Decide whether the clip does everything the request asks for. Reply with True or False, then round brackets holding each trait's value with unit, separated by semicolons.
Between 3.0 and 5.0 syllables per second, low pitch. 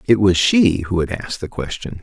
False (5.3 syllables/s; 105 Hz)